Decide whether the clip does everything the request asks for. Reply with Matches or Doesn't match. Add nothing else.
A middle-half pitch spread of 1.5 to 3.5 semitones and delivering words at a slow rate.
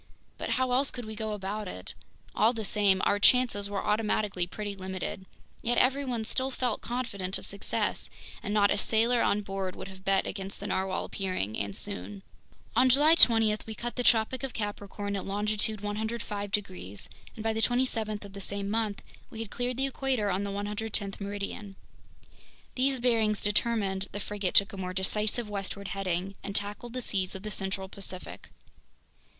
Doesn't match